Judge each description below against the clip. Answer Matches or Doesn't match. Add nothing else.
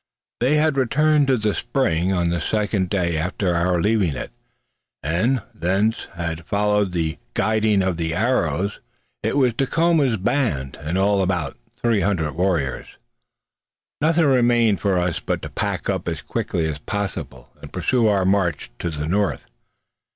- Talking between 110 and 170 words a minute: Matches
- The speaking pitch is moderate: Doesn't match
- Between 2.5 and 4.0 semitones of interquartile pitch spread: Doesn't match